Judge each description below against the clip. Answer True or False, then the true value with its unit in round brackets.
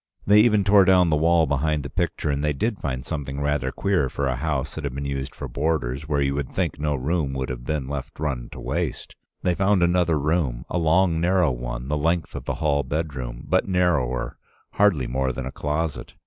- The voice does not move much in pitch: False (4.0 semitones)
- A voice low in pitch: True (75 Hz)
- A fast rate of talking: True (220 wpm)